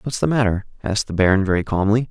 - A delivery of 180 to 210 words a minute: No, fast, 230 wpm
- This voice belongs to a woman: No, male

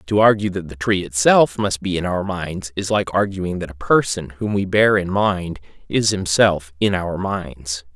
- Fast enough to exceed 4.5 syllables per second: No, 4.3 syllables/s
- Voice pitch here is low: Yes, very low, 95 Hz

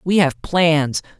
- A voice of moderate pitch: Yes, medium, 160 Hz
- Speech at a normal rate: Yes, average, 150 wpm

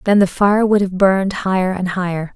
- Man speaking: No, female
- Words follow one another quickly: Yes, fast, 230 wpm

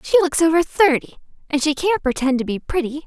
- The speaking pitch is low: No, very high, 305 Hz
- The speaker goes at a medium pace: No, fast, 215 wpm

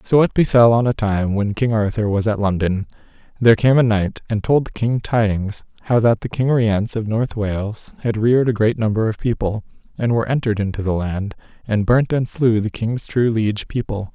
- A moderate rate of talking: No, fast, 215 wpm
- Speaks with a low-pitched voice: Yes, low, 110 Hz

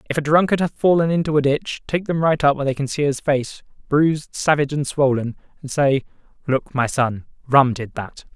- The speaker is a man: Yes, male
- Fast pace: Yes, fast, 215 wpm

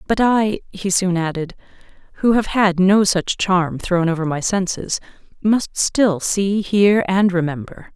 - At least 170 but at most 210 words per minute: No, average, 160 wpm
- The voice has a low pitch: No, high, 190 Hz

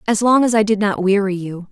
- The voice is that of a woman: Yes, female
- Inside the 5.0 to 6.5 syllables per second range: Yes, 5.8 syllables/s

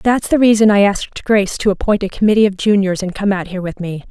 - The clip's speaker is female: Yes, female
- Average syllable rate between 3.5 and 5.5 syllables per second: No, 6.4 syllables/s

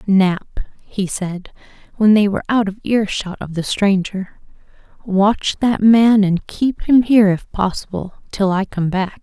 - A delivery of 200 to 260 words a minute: No, average, 170 wpm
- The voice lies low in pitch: No, high, 200 Hz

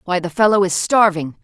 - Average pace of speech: No, fast, 210 wpm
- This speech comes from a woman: Yes, female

